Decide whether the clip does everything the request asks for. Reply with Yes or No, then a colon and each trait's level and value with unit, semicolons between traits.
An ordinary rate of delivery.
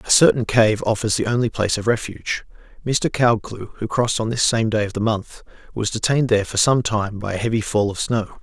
No: fast, 230 wpm